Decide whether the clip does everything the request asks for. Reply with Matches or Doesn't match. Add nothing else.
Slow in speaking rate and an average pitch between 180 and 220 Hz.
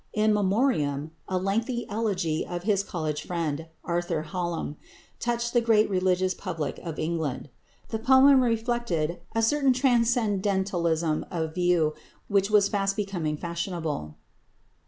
Matches